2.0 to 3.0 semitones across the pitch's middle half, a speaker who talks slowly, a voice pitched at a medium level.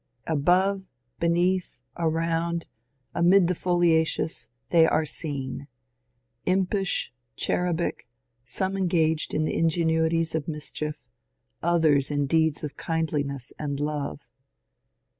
Yes: narrow, 2.6 semitones; slow, 105 wpm; medium, 160 Hz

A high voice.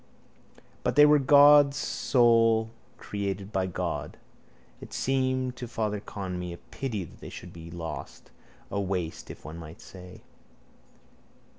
No: low, 105 Hz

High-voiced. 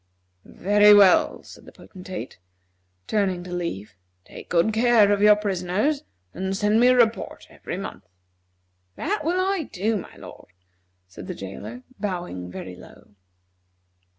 Yes: high, 200 Hz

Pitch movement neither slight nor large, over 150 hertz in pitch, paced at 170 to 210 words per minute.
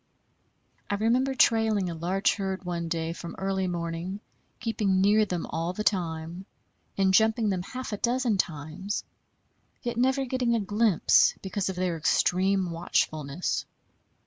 No: average, 4.1 semitones; high, 190 Hz; average, 145 wpm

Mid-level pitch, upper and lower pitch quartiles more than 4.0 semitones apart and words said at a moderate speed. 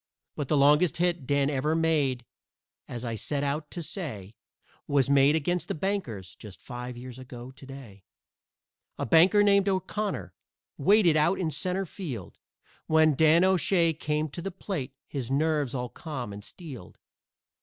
Yes: medium, 150 Hz; average, 5.0 semitones; average, 155 wpm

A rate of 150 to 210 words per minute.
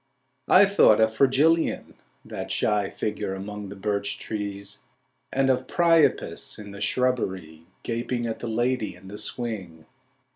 No: average, 140 wpm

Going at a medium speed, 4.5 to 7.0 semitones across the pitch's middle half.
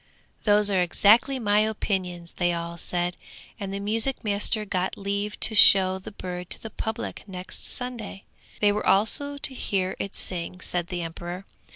No: average, 170 wpm; average, 2.9 semitones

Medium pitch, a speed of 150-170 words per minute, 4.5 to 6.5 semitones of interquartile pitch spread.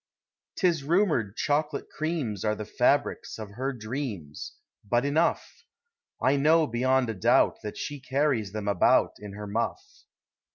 No: low, 130 Hz; average, 155 wpm; wide, 5.6 semitones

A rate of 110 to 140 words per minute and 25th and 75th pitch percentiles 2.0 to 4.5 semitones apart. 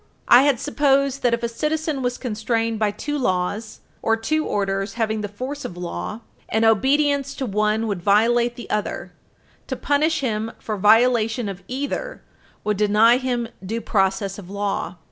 No: average, 165 wpm; average, 4.0 semitones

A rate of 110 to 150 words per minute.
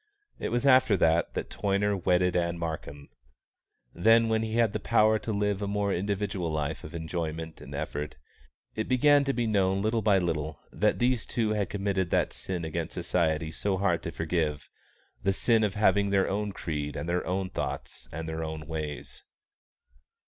No: average, 180 wpm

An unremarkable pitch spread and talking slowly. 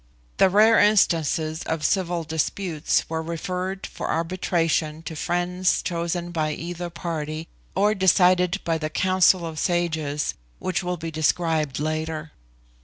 No: narrow, 2.3 semitones; slow, 130 wpm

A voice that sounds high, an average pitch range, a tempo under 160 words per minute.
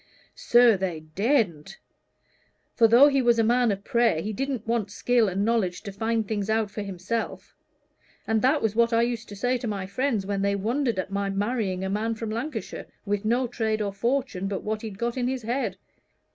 No: high, 220 Hz; average, 3.2 semitones; average, 200 wpm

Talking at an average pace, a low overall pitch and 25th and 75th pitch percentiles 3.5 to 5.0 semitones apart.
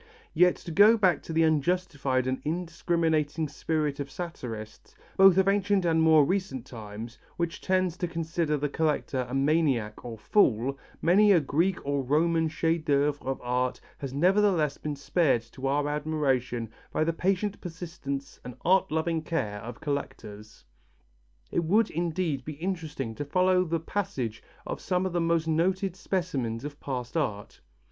No: average, 160 wpm; medium, 155 Hz; average, 4.5 semitones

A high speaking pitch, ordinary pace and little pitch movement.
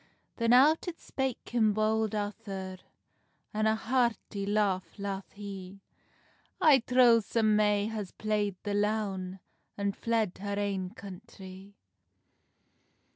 No: high, 210 Hz; slow, 120 wpm; narrow, 2.2 semitones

